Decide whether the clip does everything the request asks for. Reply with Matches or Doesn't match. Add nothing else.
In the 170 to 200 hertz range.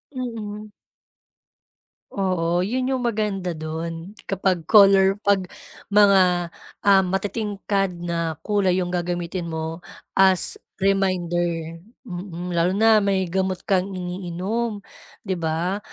Matches